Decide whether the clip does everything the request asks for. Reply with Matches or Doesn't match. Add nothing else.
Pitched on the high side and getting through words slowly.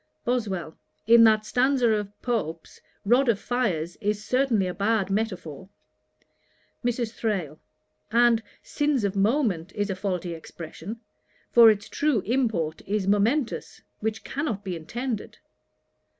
Matches